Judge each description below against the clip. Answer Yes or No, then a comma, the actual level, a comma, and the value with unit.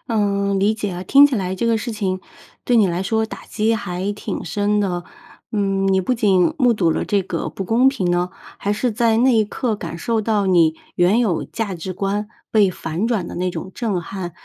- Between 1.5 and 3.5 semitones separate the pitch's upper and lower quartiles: Yes, average, 3.2 semitones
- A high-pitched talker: Yes, high, 205 Hz